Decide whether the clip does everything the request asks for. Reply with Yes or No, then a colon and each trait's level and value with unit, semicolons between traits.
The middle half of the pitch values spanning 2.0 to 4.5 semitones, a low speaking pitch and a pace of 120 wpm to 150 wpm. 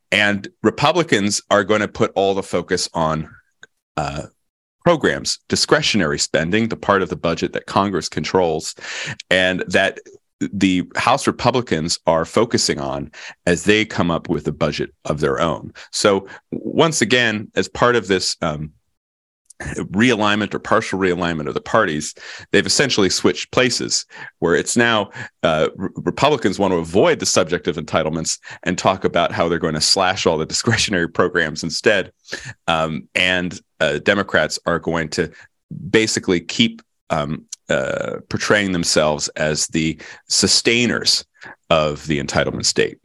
No: average, 4.9 semitones; very low, 95 Hz; average, 145 wpm